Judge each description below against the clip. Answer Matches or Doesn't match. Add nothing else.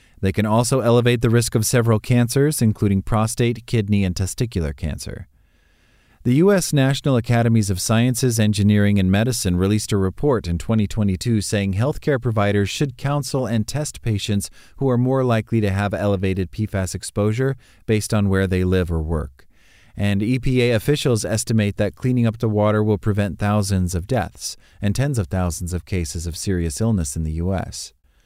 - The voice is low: Matches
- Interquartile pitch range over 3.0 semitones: Matches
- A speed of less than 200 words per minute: Matches